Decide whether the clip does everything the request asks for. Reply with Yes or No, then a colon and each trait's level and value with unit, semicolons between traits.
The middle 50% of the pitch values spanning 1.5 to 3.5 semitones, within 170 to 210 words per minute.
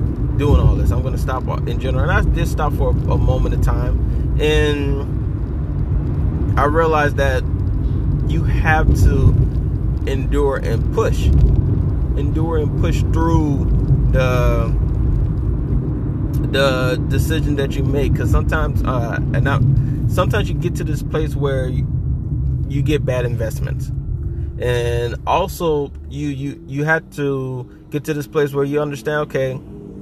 No: average, 2.9 semitones; average, 140 wpm